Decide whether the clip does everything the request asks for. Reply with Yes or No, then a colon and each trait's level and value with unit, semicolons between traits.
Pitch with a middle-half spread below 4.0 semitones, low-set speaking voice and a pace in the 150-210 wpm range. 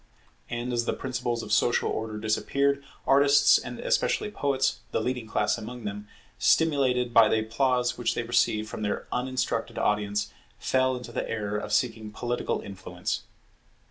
Yes: average, 3.1 semitones; low, 120 Hz; average, 155 wpm